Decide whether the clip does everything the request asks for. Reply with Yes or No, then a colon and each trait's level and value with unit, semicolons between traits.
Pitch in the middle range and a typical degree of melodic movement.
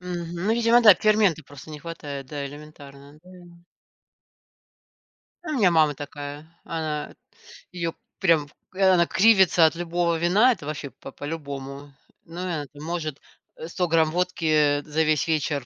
Yes: medium, 160 Hz; average, 3.3 semitones